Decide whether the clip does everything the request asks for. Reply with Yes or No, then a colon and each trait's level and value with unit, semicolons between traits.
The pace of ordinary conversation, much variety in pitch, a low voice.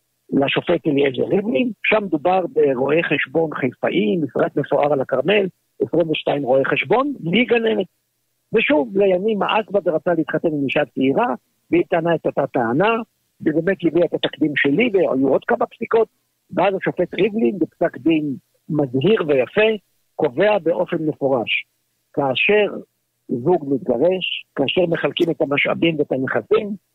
No: average, 130 wpm; wide, 5.7 semitones; medium, 170 Hz